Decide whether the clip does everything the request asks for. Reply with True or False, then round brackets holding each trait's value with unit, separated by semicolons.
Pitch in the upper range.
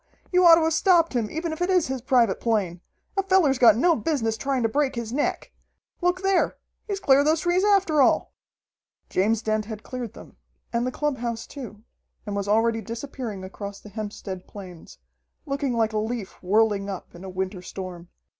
True (235 Hz)